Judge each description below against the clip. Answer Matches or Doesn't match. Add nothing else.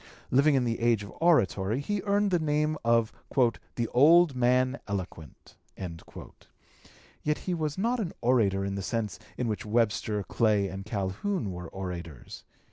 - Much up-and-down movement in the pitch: Matches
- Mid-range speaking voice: Doesn't match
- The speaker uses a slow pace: Doesn't match